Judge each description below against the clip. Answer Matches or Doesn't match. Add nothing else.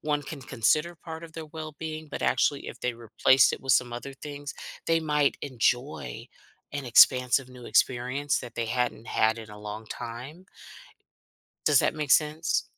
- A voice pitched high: Doesn't match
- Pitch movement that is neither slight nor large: Matches